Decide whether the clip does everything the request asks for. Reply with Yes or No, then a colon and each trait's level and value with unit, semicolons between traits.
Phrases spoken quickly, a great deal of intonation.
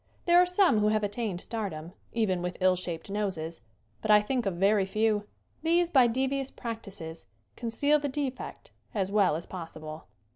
No: average, 170 wpm; wide, 5.8 semitones